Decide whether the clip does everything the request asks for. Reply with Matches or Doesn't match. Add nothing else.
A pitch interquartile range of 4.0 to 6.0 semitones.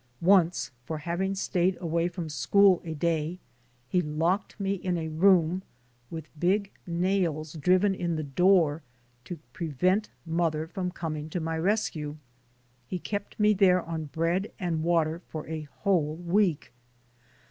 Doesn't match